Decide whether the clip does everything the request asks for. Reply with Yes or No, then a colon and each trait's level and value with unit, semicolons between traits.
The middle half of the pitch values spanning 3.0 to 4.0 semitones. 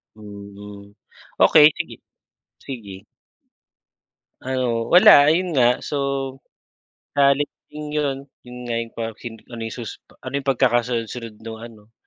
Yes: average, 3.5 semitones